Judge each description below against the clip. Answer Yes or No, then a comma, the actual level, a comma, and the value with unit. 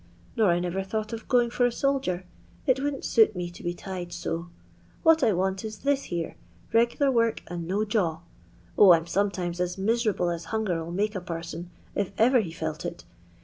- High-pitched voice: Yes, high, 195 Hz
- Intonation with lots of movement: No, average, 4.8 semitones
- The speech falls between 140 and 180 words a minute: No, average, 200 wpm